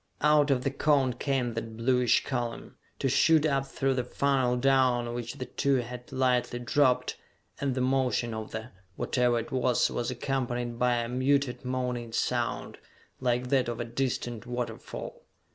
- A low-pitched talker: Yes, low, 125 Hz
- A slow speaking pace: No, average, 160 wpm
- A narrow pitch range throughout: Yes, narrow, 1.8 semitones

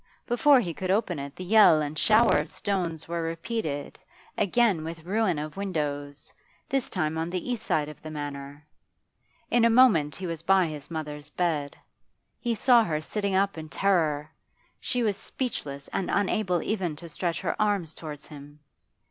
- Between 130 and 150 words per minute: No, average, 175 wpm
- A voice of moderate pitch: Yes, medium, 170 Hz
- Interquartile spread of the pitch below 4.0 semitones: No, average, 5.1 semitones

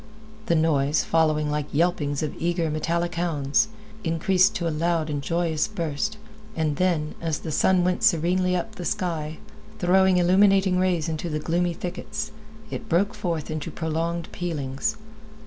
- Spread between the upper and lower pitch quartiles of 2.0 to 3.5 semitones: Yes, average, 2.7 semitones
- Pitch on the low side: No, medium, 170 Hz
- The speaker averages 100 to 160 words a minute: Yes, average, 155 wpm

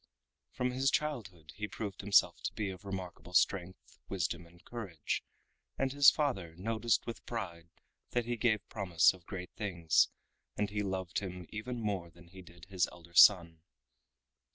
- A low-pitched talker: Yes, very low, 95 Hz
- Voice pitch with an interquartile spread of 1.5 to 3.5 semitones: No, average, 4.0 semitones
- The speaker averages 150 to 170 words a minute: Yes, average, 160 wpm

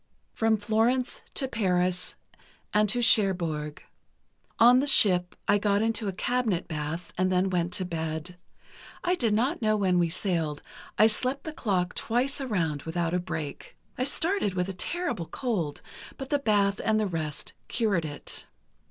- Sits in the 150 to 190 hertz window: No, high, 200 Hz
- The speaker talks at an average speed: Yes, average, 165 wpm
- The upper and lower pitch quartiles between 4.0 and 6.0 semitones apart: Yes, average, 5.0 semitones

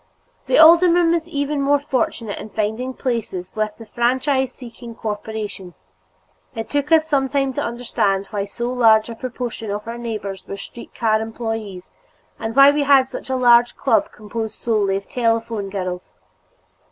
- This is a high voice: Yes, high, 230 Hz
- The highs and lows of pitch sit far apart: No, average, 3.6 semitones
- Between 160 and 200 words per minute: Yes, average, 165 wpm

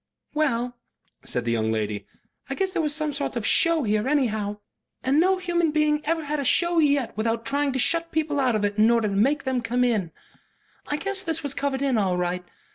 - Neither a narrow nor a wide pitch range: No, wide, 5.9 semitones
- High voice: Yes, very high, 275 Hz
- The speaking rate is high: Yes, fast, 220 wpm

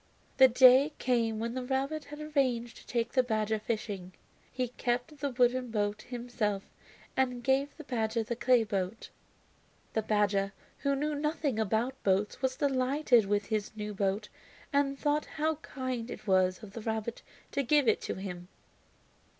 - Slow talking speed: No, average, 165 wpm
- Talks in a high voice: Yes, high, 240 Hz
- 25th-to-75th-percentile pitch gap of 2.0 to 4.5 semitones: Yes, average, 3.9 semitones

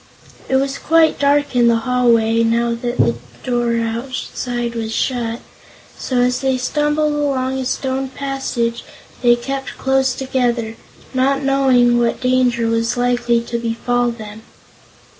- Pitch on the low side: No, high, 245 Hz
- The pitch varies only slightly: Yes, narrow, 2.2 semitones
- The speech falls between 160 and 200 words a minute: No, average, 140 wpm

